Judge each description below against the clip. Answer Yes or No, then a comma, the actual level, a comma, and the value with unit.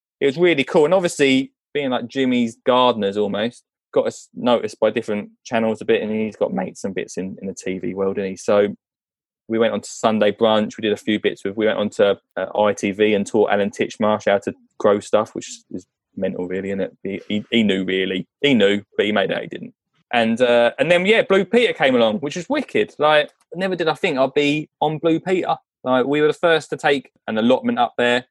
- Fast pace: Yes, fast, 235 wpm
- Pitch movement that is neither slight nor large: No, wide, 6.5 semitones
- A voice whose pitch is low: Yes, low, 120 Hz